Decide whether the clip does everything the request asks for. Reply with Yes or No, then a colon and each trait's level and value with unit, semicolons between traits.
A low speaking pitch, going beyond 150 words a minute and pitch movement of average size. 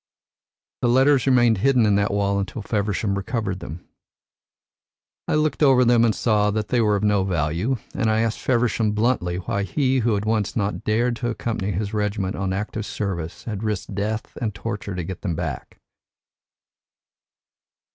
Yes: low, 105 Hz; average, 165 wpm; average, 3.0 semitones